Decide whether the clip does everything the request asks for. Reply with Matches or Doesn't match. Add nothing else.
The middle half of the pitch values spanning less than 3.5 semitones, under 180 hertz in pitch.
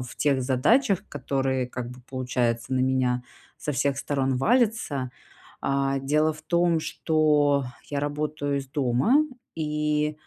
Matches